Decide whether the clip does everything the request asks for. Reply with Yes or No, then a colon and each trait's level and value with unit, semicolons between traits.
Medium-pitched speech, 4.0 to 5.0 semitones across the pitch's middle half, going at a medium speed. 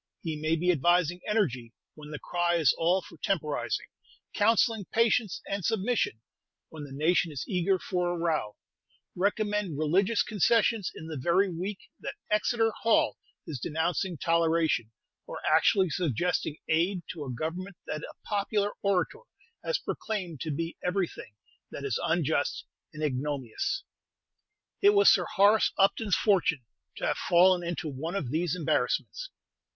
Yes: medium, 175 Hz; average, 4.4 semitones; average, 145 wpm